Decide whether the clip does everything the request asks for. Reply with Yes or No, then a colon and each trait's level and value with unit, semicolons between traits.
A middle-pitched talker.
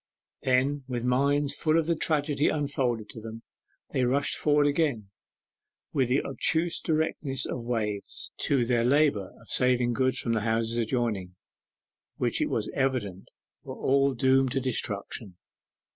No: low, 130 Hz